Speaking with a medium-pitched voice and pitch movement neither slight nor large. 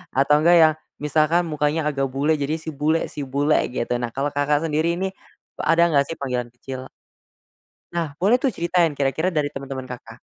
Yes: medium, 150 Hz; average, 3.1 semitones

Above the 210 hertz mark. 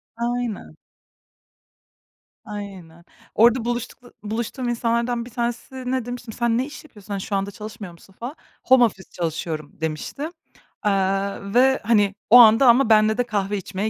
Yes: high, 225 Hz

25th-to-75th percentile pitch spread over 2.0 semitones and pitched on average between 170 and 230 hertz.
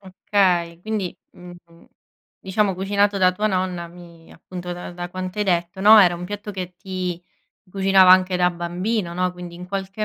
No: narrow, 1.7 semitones; medium, 185 Hz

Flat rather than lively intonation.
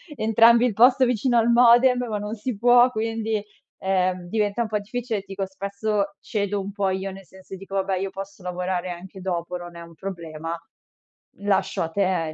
No: average, 3.2 semitones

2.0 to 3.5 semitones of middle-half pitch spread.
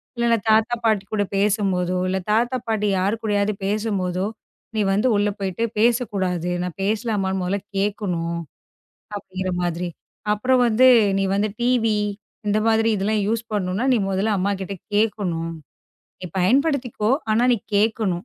Yes: average, 2.9 semitones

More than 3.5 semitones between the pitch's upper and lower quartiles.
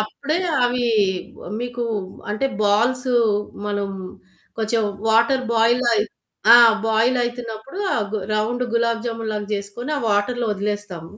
No: average, 2.7 semitones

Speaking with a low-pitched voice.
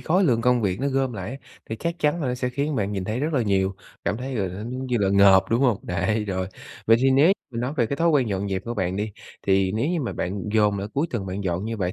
Yes: low, 110 Hz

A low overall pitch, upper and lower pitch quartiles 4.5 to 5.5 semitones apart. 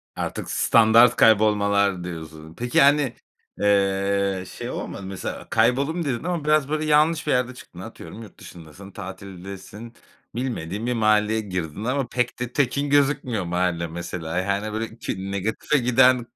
Yes: low, 110 Hz; average, 4.8 semitones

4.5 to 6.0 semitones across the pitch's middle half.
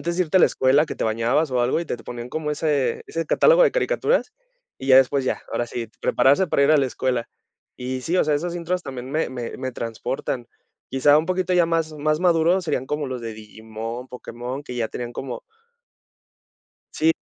Yes: average, 4.8 semitones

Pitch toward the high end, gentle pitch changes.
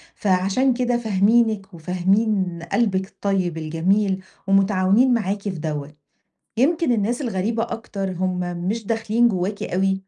No: high, 195 Hz; average, 3.4 semitones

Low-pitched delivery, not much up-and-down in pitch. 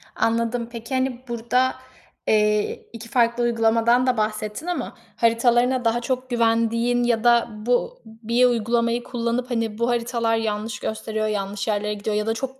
No: high, 230 Hz; narrow, 1.6 semitones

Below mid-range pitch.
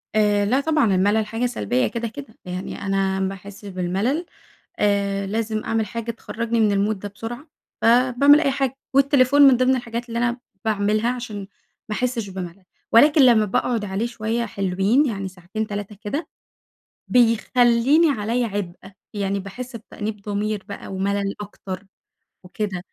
No: high, 215 Hz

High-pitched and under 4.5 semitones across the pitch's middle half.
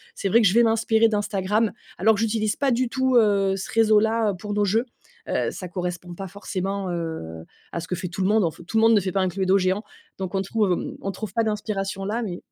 Yes: high, 200 Hz; average, 3.0 semitones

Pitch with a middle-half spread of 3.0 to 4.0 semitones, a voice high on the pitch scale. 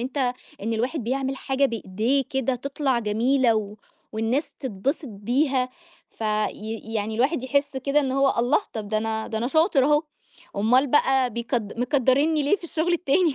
Yes: average, 3.7 semitones; very high, 260 Hz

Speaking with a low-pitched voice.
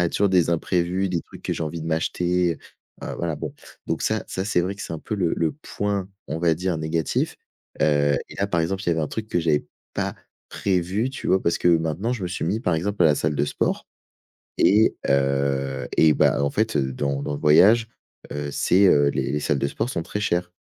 Yes: very low, 85 Hz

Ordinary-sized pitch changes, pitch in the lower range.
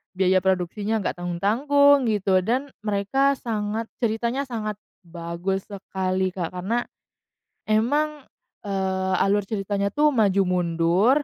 No: average, 3.8 semitones; high, 200 Hz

